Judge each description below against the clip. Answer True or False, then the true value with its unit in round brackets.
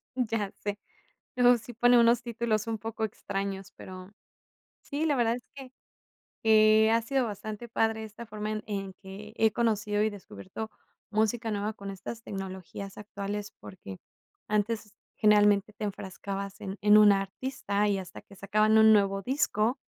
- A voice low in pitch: False (215 Hz)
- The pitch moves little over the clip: True (2.1 semitones)